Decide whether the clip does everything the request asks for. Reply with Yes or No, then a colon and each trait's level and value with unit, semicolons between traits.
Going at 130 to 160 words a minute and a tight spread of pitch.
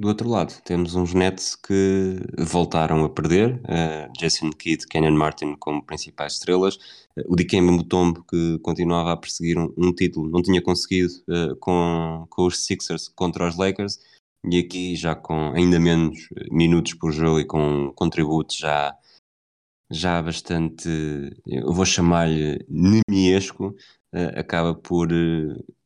Yes: average, 145 wpm; narrow, 2.2 semitones